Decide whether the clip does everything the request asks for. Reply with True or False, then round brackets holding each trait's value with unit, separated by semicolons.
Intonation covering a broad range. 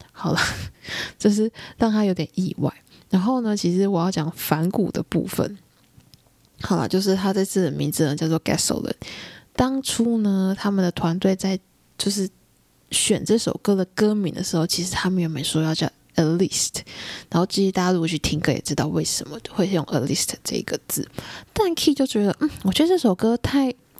False (3.9 semitones)